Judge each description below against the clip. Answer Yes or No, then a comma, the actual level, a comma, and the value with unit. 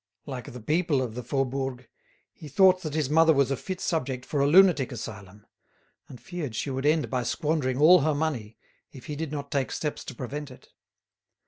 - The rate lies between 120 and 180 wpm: No, average, 200 wpm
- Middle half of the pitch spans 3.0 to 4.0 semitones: Yes, average, 3.7 semitones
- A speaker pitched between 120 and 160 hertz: Yes, medium, 140 Hz